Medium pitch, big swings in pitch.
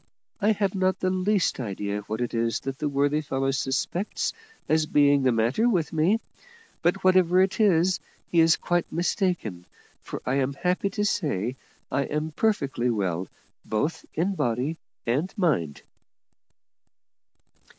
Yes: medium, 155 Hz; wide, 6.7 semitones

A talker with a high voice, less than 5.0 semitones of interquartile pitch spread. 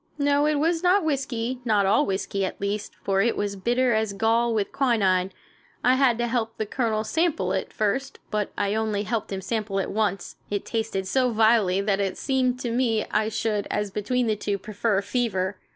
Yes: high, 220 Hz; average, 3.6 semitones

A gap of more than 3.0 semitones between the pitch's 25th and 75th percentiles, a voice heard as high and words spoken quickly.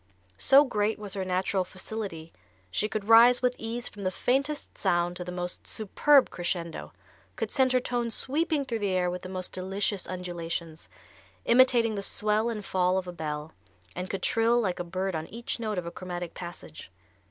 No: average, 4.5 semitones; high, 195 Hz; average, 185 wpm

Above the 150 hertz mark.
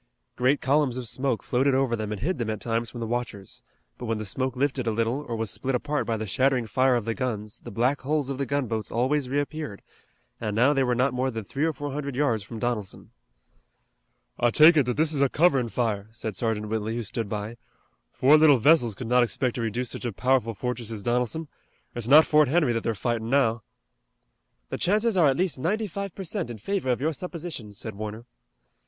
No: low, 125 Hz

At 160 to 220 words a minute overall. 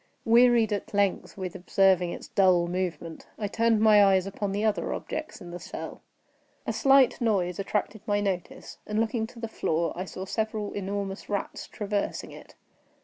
Yes: average, 170 wpm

